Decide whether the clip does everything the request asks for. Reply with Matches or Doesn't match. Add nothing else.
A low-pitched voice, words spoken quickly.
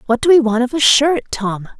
Doesn't match